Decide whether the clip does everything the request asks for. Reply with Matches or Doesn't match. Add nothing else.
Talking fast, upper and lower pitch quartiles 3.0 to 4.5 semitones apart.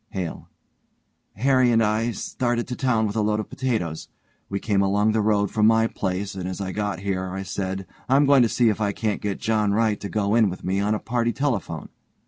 Doesn't match